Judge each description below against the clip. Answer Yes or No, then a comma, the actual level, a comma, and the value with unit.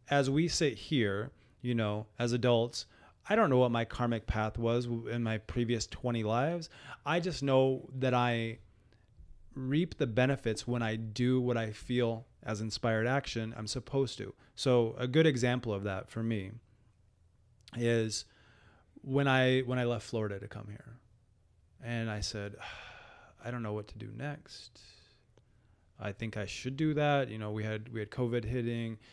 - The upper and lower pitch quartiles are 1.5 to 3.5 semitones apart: Yes, average, 2.7 semitones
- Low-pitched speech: Yes, low, 115 Hz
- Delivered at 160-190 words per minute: Yes, average, 170 wpm